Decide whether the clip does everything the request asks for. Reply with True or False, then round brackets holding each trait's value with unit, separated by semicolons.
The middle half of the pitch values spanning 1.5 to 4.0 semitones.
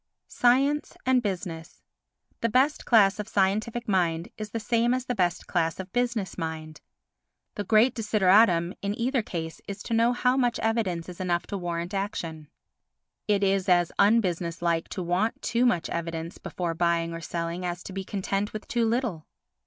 False (5.0 semitones)